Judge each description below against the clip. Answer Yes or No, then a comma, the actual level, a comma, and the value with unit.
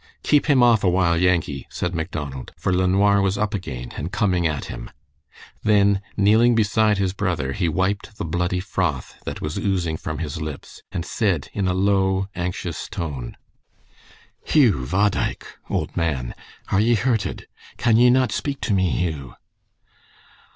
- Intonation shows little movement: No, average, 3.9 semitones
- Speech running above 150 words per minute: Yes, average, 160 wpm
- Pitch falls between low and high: No, very low, 95 Hz